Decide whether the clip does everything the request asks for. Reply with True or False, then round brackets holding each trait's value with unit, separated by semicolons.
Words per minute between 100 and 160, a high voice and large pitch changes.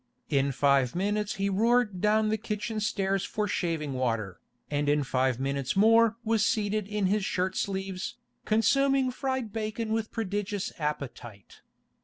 True (145 wpm; 200 Hz; 6.7 semitones)